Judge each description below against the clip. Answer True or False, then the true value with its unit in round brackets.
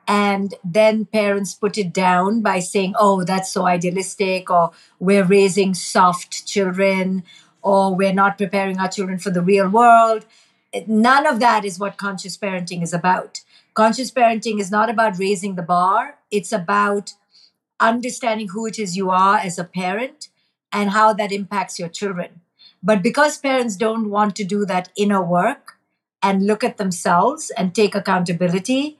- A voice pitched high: True (200 Hz)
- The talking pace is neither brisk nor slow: True (160 wpm)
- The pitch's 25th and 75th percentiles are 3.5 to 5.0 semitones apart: False (2.7 semitones)